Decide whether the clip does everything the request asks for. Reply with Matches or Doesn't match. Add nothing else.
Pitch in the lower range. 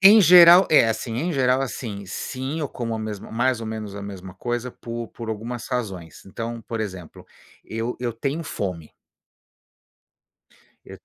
Matches